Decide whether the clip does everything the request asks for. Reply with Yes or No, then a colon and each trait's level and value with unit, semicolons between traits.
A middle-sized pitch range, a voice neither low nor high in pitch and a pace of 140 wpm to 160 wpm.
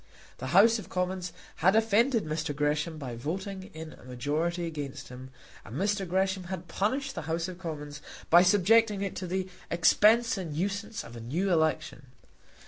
No: average, 4.5 semitones; medium, 175 Hz; average, 170 wpm